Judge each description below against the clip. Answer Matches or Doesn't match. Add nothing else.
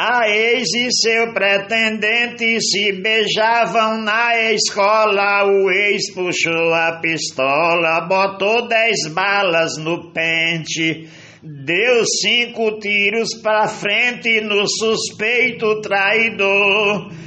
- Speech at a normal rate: Doesn't match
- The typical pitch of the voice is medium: Doesn't match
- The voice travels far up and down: Doesn't match